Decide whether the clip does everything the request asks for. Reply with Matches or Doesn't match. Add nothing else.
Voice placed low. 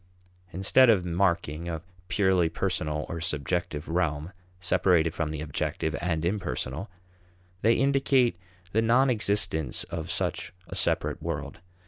Matches